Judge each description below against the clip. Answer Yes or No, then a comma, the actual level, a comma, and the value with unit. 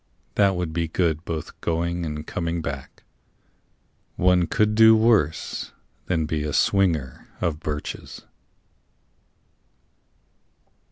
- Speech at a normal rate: No, slow, 105 wpm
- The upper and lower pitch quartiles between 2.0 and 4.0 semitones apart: Yes, average, 2.9 semitones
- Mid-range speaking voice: No, very low, 85 Hz